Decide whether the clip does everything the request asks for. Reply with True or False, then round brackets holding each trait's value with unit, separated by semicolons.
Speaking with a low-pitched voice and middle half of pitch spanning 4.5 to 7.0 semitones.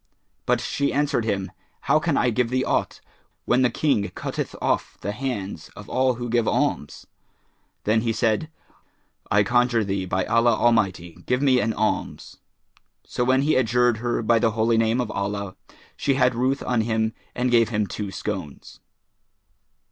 False (115 Hz; 3.1 semitones)